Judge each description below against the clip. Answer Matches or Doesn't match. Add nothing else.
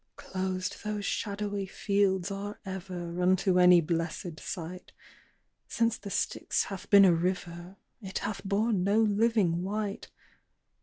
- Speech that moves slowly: Matches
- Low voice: Doesn't match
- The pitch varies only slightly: Matches